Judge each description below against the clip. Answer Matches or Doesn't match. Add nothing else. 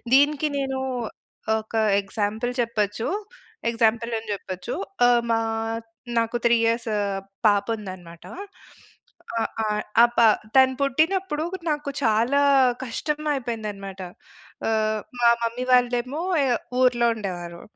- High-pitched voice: Matches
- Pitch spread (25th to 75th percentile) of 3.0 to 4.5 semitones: Matches